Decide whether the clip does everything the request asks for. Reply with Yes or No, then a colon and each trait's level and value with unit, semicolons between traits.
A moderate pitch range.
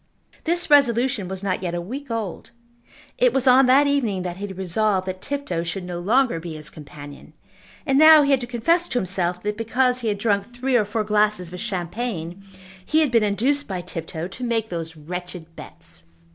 No: wide, 6.0 semitones